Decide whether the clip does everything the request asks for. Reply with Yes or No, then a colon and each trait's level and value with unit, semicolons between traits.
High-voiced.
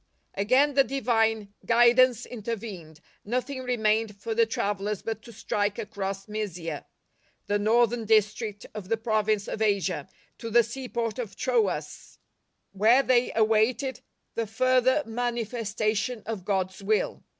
Yes: high, 220 Hz